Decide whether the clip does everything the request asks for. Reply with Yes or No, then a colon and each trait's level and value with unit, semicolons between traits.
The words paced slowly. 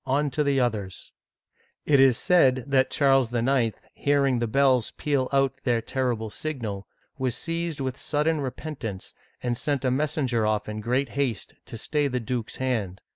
No: average, 170 wpm